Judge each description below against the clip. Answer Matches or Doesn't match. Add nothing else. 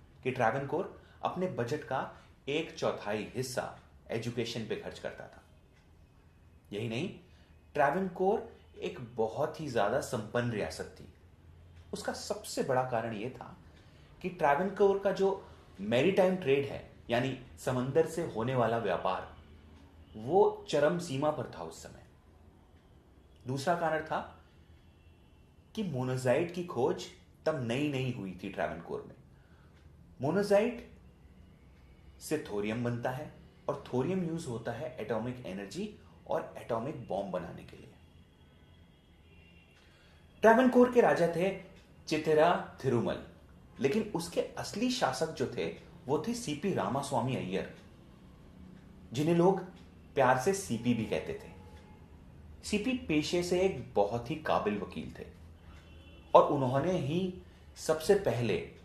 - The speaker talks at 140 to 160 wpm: Doesn't match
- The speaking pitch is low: Matches